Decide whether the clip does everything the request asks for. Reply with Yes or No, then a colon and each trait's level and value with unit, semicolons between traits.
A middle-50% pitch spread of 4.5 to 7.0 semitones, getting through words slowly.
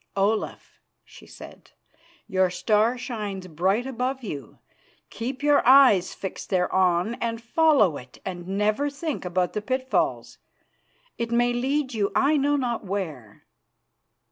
Yes: wide, 5.6 semitones; slow, 130 wpm